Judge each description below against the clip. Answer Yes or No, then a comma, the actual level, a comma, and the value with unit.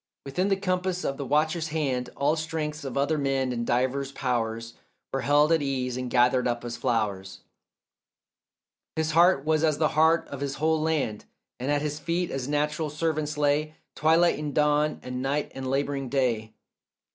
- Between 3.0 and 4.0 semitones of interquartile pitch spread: Yes, average, 3.3 semitones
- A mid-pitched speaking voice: Yes, medium, 145 Hz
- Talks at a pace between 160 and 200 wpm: Yes, average, 175 wpm